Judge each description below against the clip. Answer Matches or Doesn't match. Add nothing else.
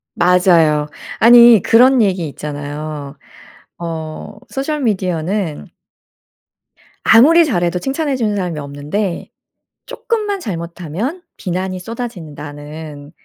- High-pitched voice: Doesn't match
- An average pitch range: Doesn't match